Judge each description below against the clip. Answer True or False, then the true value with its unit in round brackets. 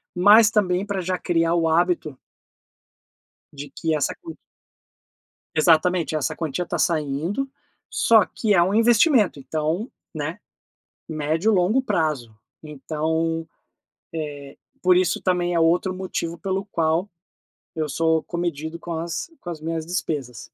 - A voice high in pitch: False (170 Hz)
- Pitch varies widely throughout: False (2.9 semitones)